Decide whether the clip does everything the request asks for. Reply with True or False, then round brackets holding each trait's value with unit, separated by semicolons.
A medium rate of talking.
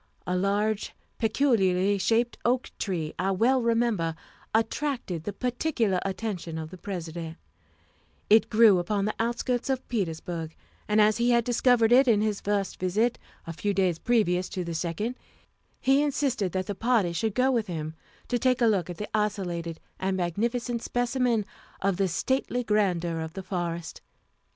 True (160 wpm)